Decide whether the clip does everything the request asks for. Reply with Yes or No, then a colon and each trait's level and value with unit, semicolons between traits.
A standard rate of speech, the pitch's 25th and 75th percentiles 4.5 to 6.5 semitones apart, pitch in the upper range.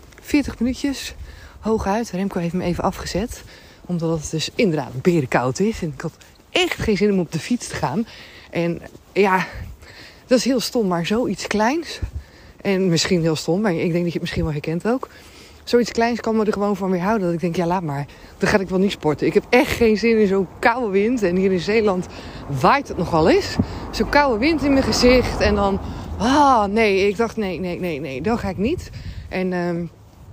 No: fast, 220 wpm; average, 4.8 semitones; high, 195 Hz